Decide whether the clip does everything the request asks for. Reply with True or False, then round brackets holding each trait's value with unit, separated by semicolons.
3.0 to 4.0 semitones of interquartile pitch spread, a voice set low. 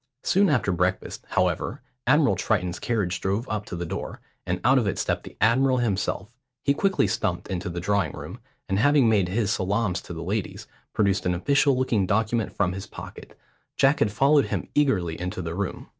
False (5.6 semitones; 105 Hz)